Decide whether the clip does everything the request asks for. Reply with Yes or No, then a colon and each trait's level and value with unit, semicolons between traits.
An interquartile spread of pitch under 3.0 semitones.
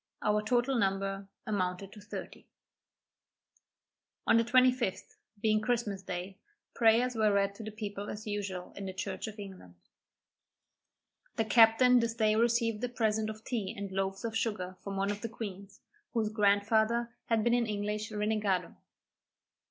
Yes: narrow, 2.4 semitones